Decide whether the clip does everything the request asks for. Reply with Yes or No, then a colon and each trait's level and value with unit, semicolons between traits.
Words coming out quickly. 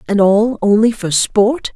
No: average, 170 wpm